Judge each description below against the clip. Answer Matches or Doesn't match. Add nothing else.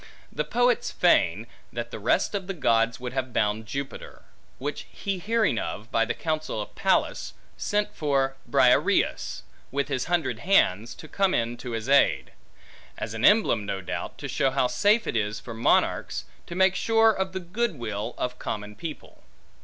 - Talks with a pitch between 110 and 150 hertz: Matches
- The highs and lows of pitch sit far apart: Matches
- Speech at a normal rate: Matches